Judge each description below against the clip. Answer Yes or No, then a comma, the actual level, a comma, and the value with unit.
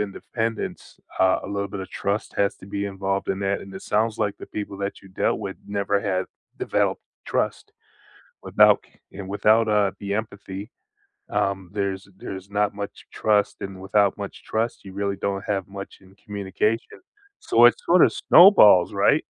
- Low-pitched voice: Yes, low, 100 Hz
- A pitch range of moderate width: No, narrow, 1.3 semitones